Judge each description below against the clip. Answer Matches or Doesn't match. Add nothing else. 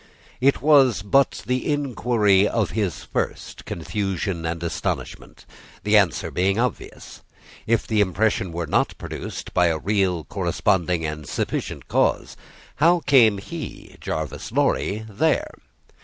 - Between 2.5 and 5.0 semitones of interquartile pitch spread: Doesn't match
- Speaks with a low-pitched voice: Matches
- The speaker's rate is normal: Doesn't match